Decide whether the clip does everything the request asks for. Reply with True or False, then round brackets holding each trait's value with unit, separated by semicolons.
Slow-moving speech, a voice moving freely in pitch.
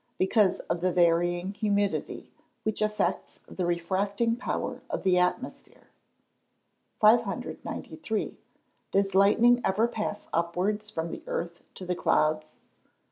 False (120 wpm; 3.4 semitones)